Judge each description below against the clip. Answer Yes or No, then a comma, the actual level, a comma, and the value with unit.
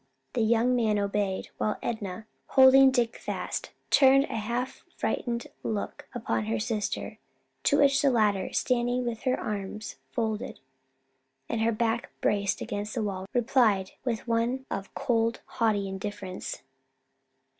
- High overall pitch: Yes, high, 225 Hz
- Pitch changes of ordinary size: Yes, average, 3.1 semitones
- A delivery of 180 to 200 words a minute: No, slow, 135 wpm